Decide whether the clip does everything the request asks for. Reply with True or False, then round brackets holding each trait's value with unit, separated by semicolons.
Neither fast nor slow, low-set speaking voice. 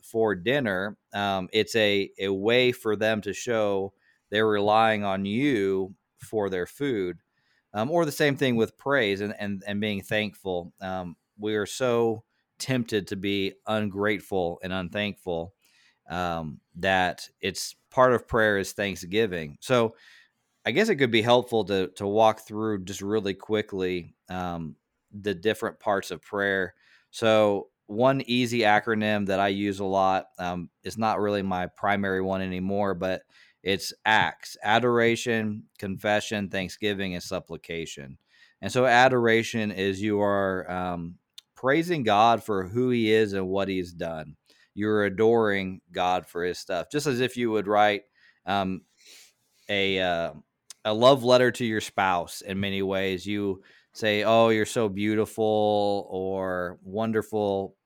True (145 wpm; 100 Hz)